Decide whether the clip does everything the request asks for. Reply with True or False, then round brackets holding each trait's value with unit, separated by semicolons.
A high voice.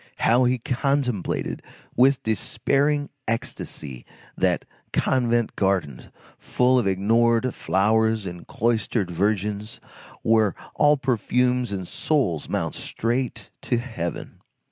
False (115 Hz)